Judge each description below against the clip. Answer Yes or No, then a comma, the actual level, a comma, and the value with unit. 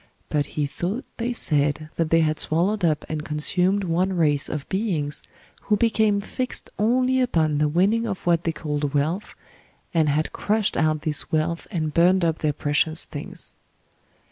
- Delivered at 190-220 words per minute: No, average, 170 wpm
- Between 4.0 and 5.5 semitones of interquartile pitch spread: Yes, average, 4.8 semitones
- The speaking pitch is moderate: Yes, medium, 165 Hz